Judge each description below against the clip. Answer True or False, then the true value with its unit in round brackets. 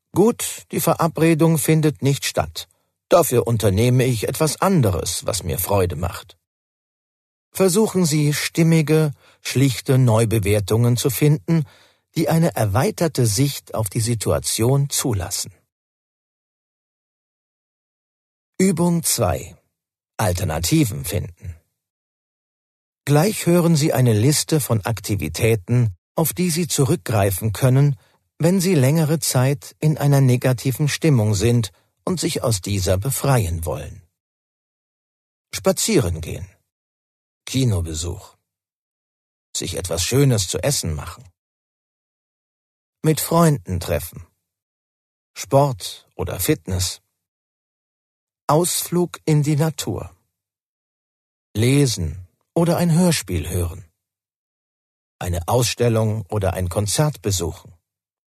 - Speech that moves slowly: True (95 wpm)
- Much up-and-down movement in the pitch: True (8.6 semitones)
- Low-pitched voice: True (120 Hz)